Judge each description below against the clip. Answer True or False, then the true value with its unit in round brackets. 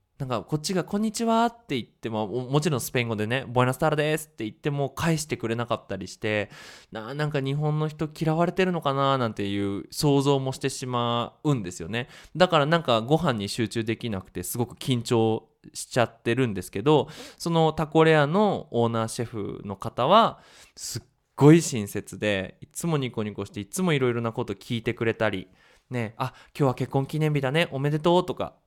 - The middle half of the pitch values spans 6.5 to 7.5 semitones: False (5.5 semitones)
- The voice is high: False (130 Hz)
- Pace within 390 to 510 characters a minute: True (400 characters per minute)